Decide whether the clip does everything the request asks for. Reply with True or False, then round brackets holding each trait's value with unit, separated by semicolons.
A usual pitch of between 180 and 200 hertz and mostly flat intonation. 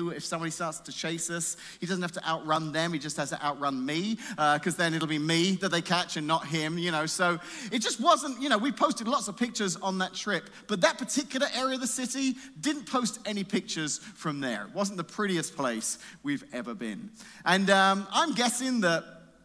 False (185 Hz; 7.0 semitones)